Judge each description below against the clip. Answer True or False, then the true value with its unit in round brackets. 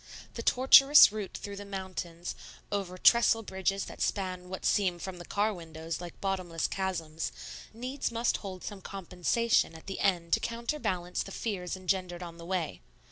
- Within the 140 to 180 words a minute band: True (165 wpm)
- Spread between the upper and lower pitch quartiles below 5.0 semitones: True (2.7 semitones)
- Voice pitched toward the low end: False (190 Hz)